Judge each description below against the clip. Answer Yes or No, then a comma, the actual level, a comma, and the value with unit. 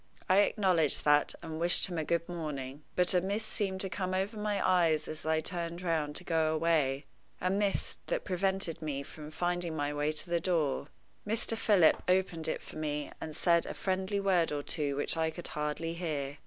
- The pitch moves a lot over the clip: No, average, 3.4 semitones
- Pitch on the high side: No, medium, 170 Hz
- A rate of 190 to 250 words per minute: Yes, average, 195 wpm